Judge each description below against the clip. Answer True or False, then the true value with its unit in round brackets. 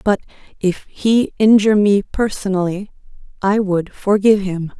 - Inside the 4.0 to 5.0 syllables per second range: True (4.6 syllables/s)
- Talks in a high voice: True (200 Hz)